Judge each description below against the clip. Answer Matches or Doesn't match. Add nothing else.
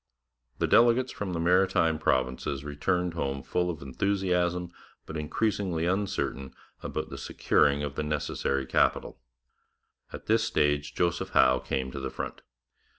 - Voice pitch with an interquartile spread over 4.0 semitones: Matches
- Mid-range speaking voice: Doesn't match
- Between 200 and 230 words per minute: Doesn't match